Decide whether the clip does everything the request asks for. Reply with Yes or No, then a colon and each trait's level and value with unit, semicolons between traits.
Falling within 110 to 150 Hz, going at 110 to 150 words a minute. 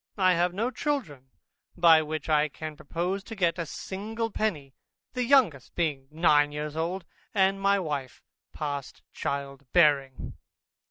No: medium, 165 Hz; average, 145 wpm